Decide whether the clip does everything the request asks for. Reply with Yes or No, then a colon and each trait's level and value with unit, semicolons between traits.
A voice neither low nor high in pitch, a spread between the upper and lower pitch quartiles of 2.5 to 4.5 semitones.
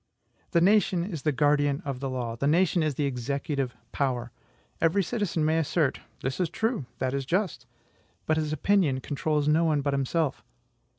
Yes: medium, 150 Hz; average, 3.7 semitones